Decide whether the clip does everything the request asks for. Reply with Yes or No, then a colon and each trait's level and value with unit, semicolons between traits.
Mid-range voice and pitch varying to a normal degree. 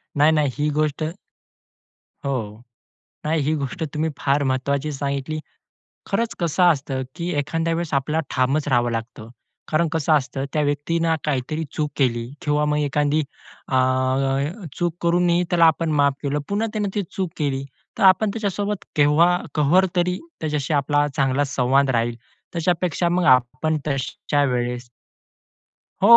Yes: medium, 150 Hz; average, 3.5 semitones